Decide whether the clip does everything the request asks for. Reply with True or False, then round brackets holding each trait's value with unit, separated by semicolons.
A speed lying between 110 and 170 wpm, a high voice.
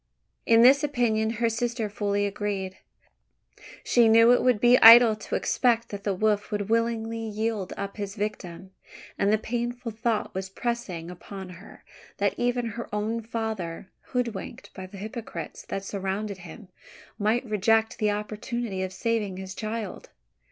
True (150 wpm; 215 Hz)